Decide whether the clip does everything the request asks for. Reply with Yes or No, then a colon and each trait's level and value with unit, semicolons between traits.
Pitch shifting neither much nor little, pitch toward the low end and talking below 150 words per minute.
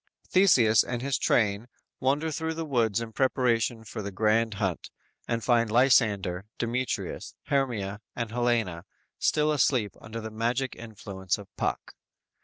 Yes: average, 3.2 semitones; low, 115 Hz; average, 140 wpm